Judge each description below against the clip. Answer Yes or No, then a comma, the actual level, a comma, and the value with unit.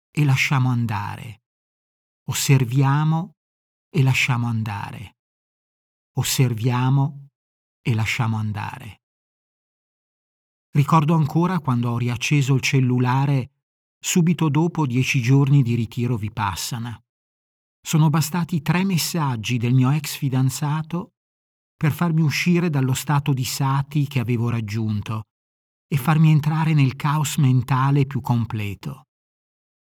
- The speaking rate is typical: No, slow, 105 wpm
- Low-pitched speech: Yes, low, 130 Hz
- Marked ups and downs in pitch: No, average, 4.2 semitones